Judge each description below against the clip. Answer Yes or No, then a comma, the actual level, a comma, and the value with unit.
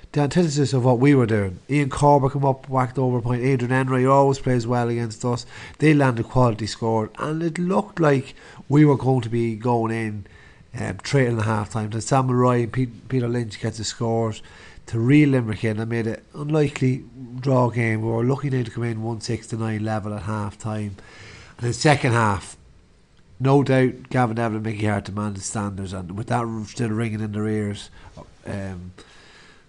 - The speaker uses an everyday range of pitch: Yes, average, 3.3 semitones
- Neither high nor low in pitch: No, low, 120 Hz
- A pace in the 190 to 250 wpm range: Yes, average, 195 wpm